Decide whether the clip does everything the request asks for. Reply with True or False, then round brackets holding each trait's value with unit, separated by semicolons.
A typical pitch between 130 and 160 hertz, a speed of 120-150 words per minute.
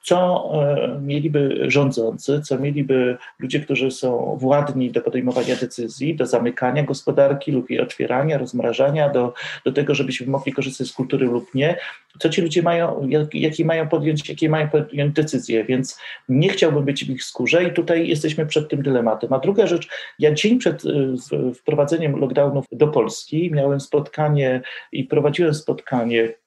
False (140 Hz; 160 wpm)